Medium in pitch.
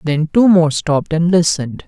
Yes: medium, 165 Hz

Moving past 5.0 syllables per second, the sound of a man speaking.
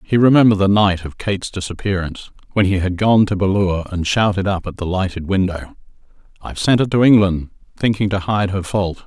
Yes: 5.9 syllables/s; male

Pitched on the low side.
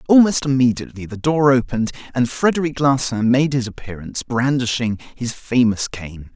Yes: low, 125 Hz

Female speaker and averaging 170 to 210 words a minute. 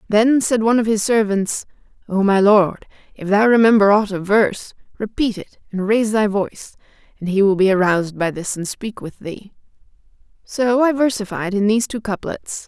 Yes: female; average, 185 wpm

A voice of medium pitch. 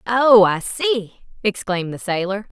No: high, 210 Hz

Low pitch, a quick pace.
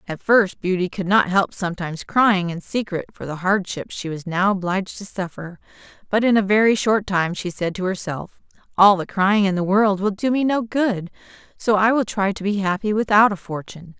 No: high, 195 Hz; fast, 215 wpm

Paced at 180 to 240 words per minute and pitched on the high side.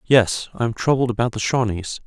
No: fast, 205 wpm; low, 120 Hz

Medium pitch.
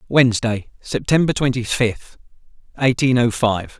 No: low, 120 Hz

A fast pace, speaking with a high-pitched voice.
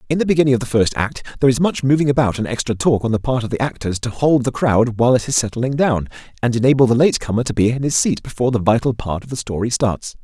No: fast, 280 wpm; low, 120 Hz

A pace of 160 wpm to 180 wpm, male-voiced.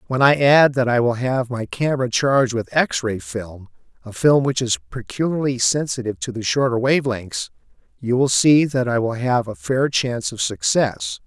No: average, 195 wpm; male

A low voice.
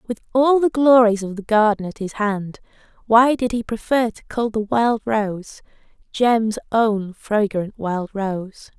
No: high, 220 Hz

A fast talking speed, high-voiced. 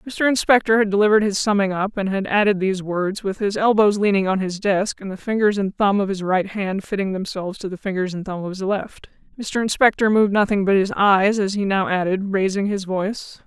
Yes: fast, 230 wpm; high, 200 Hz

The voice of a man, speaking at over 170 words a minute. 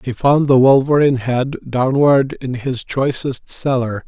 No: male; average, 145 wpm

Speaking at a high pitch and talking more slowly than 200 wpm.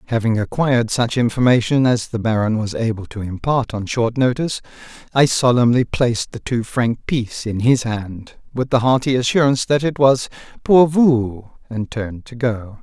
No: low, 120 Hz; average, 175 wpm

